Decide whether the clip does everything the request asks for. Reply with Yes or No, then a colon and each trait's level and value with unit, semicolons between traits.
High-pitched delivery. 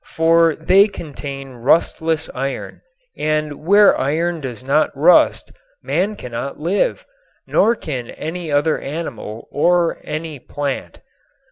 No: medium, 155 Hz